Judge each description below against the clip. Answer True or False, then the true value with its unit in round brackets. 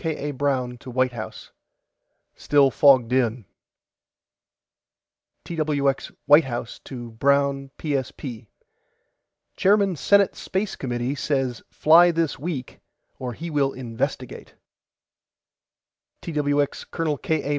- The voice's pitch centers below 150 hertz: True (140 Hz)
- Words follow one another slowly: True (105 wpm)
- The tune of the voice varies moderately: True (3.5 semitones)